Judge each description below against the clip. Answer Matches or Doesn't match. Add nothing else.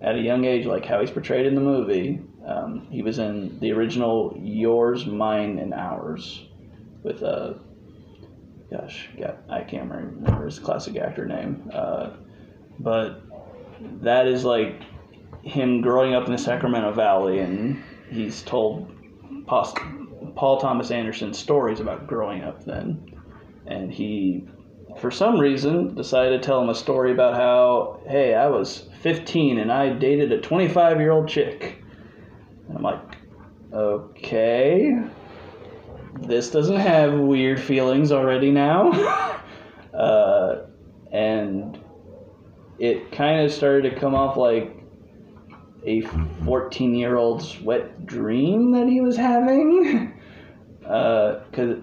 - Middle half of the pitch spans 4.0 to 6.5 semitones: Matches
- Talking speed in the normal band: Doesn't match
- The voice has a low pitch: Matches